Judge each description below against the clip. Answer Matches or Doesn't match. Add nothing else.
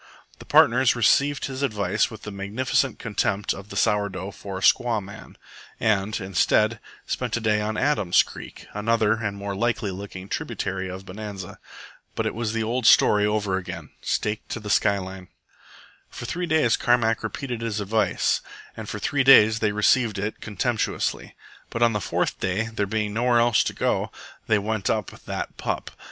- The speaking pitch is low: Matches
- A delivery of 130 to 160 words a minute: Doesn't match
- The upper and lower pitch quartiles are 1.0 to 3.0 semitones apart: Matches